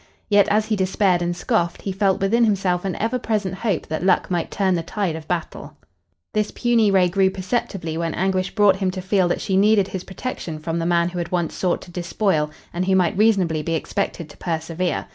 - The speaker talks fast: Yes, fast, 220 wpm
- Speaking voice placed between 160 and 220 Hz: Yes, medium, 185 Hz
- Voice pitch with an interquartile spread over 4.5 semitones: No, average, 2.7 semitones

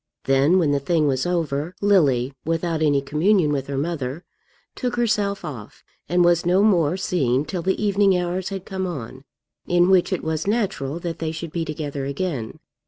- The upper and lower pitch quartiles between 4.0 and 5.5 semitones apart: Yes, average, 4.6 semitones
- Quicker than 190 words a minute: No, average, 180 wpm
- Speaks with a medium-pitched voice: Yes, medium, 165 Hz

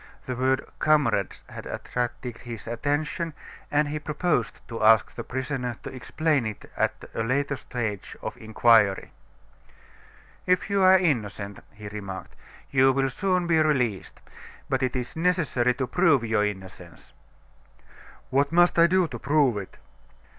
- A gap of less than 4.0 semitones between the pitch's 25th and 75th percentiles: No, wide, 5.4 semitones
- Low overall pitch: Yes, low, 130 Hz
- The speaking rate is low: No, average, 145 wpm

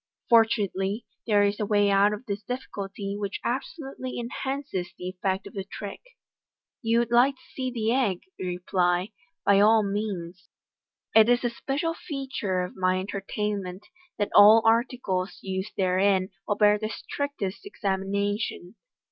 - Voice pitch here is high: Yes, high, 205 Hz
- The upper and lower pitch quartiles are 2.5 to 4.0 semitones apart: Yes, average, 3.6 semitones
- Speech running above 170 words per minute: No, average, 160 wpm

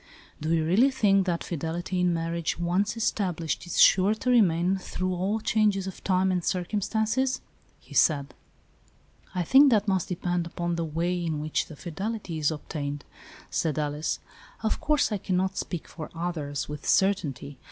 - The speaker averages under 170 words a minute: No, average, 175 wpm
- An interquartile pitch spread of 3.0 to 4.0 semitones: Yes, average, 3.5 semitones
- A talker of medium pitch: Yes, medium, 180 Hz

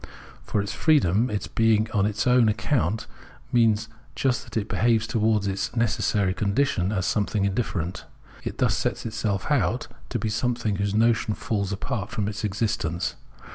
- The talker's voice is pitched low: Yes, low, 110 Hz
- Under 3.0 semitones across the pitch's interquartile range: Yes, narrow, 2.4 semitones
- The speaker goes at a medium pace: Yes, average, 160 wpm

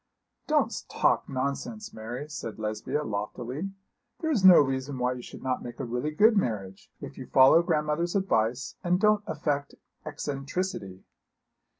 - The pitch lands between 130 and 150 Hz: Yes, medium, 140 Hz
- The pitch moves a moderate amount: No, wide, 6.2 semitones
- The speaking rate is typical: Yes, average, 150 wpm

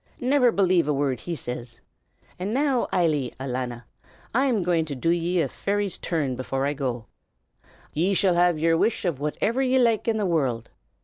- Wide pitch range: Yes, wide, 7.0 semitones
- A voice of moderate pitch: Yes, medium, 170 Hz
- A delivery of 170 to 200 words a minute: Yes, average, 180 wpm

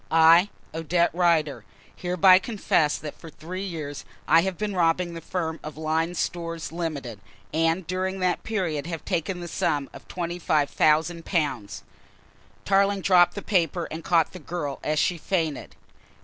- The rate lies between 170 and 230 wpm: No, average, 150 wpm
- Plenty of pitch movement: No, narrow, 2.5 semitones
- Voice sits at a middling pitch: Yes, medium, 165 Hz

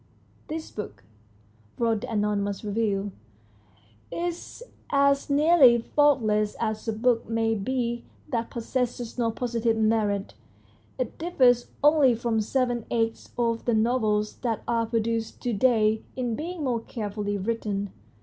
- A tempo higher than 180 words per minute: No, slow, 135 wpm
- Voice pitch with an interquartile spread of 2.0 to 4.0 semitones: Yes, average, 2.7 semitones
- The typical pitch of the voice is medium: No, high, 230 Hz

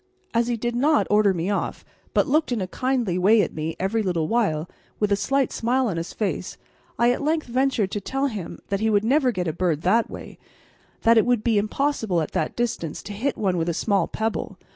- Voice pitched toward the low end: No, high, 215 Hz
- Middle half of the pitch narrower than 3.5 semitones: No, average, 4.9 semitones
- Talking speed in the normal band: No, fast, 230 wpm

